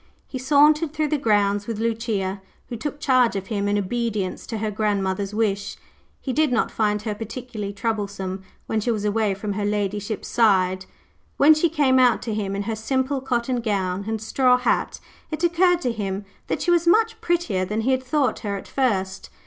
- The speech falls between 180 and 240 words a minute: Yes, average, 195 wpm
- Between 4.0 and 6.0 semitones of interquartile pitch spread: Yes, average, 4.4 semitones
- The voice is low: No, high, 220 Hz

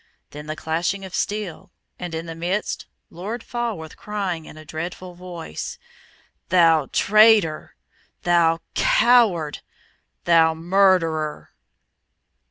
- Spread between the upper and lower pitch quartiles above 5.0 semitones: No, average, 3.6 semitones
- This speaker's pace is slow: Yes, slow, 105 wpm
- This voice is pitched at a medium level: Yes, medium, 175 Hz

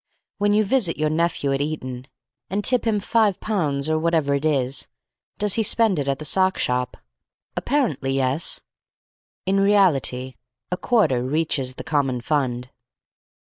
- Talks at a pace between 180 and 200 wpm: No, average, 150 wpm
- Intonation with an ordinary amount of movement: No, wide, 6.6 semitones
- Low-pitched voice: No, medium, 155 Hz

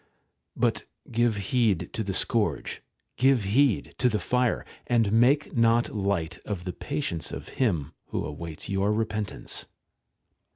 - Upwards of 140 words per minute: No, slow, 135 wpm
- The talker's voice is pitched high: No, low, 110 Hz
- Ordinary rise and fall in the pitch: Yes, average, 3.9 semitones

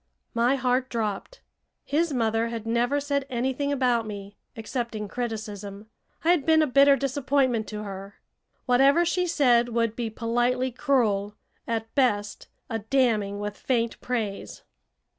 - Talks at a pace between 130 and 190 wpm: Yes, average, 140 wpm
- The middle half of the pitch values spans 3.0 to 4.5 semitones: Yes, average, 3.8 semitones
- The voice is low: No, high, 240 Hz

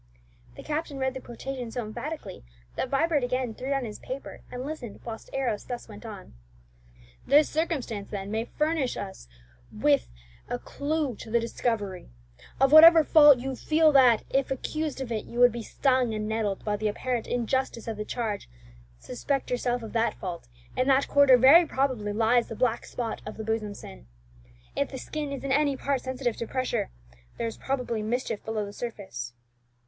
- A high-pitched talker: Yes, high, 245 Hz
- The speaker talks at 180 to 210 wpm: Yes, average, 185 wpm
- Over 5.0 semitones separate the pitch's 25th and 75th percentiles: No, average, 3.8 semitones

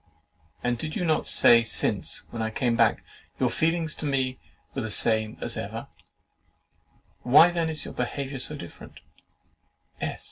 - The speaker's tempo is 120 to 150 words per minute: Yes, average, 145 wpm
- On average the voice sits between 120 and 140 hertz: Yes, low, 135 Hz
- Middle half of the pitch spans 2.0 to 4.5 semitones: No, average, 5.1 semitones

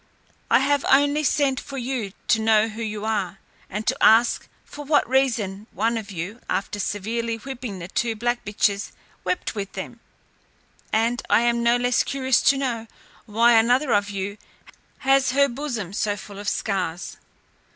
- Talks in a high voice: Yes, high, 230 Hz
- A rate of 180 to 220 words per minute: No, average, 165 wpm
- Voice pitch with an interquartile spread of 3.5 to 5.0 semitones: Yes, average, 4.0 semitones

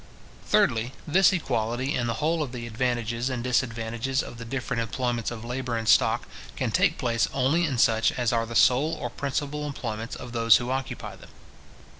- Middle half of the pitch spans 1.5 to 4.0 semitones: Yes, narrow, 2.5 semitones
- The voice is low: Yes, low, 120 Hz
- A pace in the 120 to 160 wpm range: No, average, 185 wpm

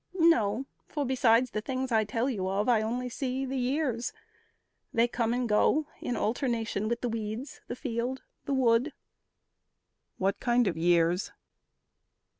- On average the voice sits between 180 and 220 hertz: No, high, 235 Hz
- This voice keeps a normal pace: Yes, average, 150 wpm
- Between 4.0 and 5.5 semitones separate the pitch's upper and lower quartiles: No, average, 3.0 semitones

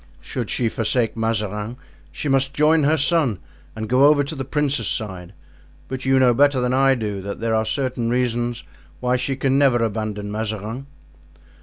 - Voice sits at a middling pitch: No, low, 125 Hz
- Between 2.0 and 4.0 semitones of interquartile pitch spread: Yes, average, 3.6 semitones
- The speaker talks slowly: No, average, 175 wpm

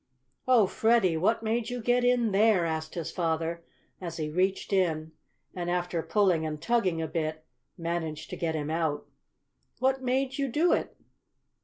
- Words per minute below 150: No, average, 165 wpm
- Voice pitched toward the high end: No, medium, 175 Hz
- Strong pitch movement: Yes, wide, 6.2 semitones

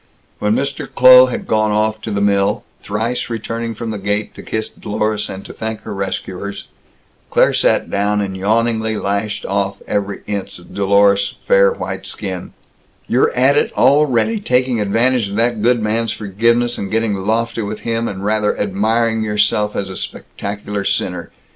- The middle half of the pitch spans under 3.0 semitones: Yes, narrow, 2.4 semitones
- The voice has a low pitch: Yes, low, 110 Hz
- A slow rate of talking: No, average, 165 wpm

